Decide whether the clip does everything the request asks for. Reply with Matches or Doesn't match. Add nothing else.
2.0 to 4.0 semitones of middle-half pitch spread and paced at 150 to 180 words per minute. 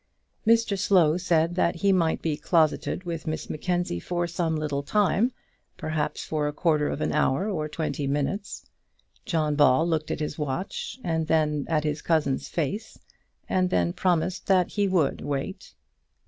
Matches